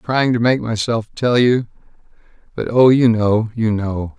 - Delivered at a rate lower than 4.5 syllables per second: Yes, 4.3 syllables/s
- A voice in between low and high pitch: No, low, 115 Hz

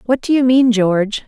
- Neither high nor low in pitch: No, high, 235 Hz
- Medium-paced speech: No, fast, 235 wpm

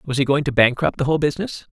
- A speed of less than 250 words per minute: No, fast, 275 wpm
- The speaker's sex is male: Yes, male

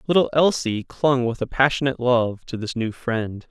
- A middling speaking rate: Yes, average, 190 wpm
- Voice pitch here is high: No, low, 125 Hz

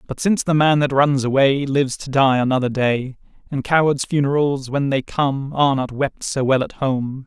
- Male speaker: Yes, male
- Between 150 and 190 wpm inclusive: No, fast, 205 wpm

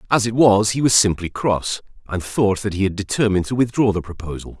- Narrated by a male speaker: Yes, male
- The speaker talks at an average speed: No, fast, 220 wpm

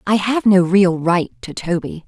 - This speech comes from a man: No, female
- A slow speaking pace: No, average, 200 wpm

